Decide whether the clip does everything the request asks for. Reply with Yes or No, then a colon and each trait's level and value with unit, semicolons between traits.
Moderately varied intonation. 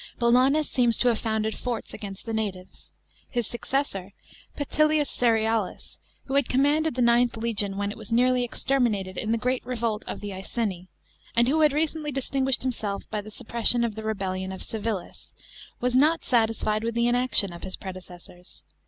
Yes: average, 3.5 semitones